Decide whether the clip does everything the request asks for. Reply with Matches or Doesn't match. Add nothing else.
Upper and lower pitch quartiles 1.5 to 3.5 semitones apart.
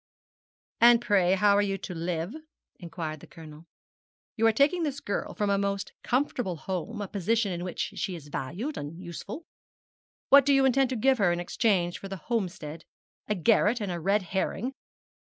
Doesn't match